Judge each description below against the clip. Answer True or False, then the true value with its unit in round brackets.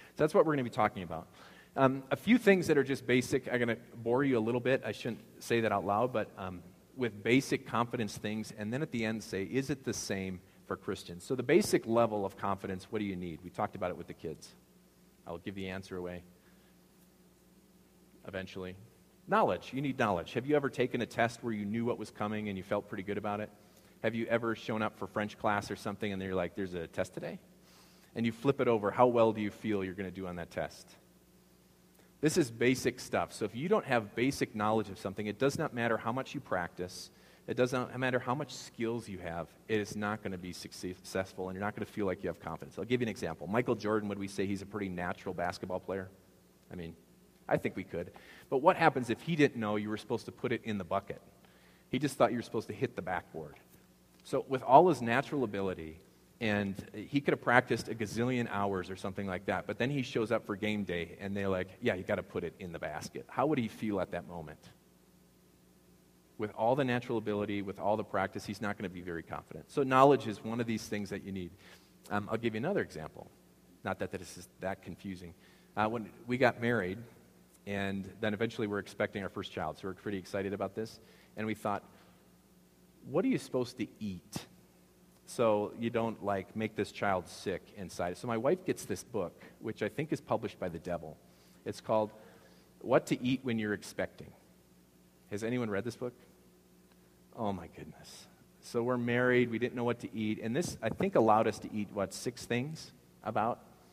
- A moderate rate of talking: False (225 wpm)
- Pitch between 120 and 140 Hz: False (105 Hz)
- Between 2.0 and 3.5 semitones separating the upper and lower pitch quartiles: False (4.3 semitones)